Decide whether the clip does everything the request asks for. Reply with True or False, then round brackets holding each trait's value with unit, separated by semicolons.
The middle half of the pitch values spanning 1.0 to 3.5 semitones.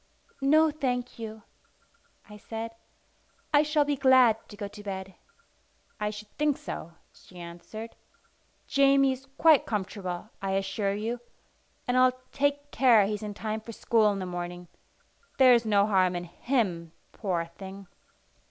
False (4.9 semitones)